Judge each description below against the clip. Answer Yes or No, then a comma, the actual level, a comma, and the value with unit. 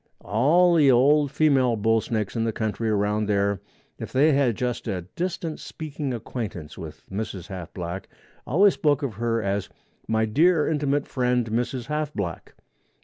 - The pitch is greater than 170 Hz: No, low, 120 Hz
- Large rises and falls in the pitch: Yes, wide, 5.8 semitones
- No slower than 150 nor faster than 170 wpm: Yes, average, 160 wpm